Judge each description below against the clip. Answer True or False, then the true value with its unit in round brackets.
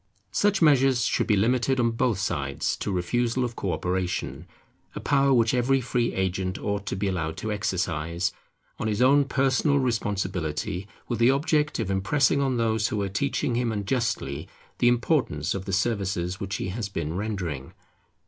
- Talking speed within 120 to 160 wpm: False (170 wpm)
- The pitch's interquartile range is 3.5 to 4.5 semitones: False (5.2 semitones)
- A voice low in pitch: True (110 Hz)